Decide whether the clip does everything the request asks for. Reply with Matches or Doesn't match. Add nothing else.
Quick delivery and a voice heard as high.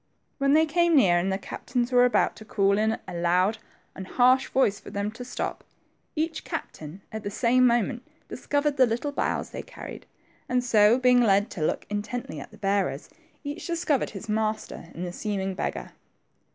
Doesn't match